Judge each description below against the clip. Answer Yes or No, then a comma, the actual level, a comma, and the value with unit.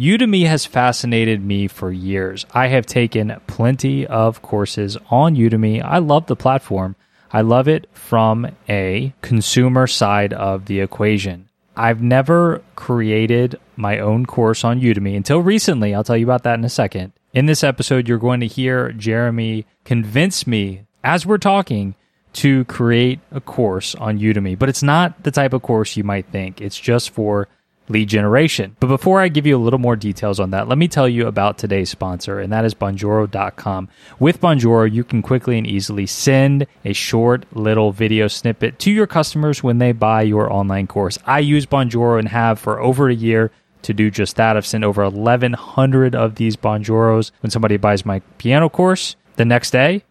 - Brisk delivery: No, average, 185 wpm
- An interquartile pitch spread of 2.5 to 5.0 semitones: Yes, average, 4.0 semitones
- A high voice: No, low, 115 Hz